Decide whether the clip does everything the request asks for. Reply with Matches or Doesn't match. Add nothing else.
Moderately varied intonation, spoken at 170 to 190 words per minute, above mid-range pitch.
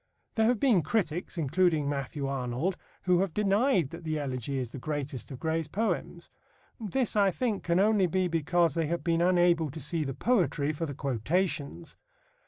Doesn't match